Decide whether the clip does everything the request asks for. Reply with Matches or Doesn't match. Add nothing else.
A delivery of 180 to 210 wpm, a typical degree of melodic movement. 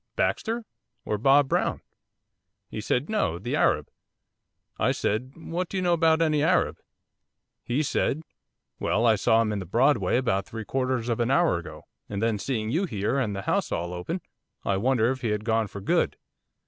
Doesn't match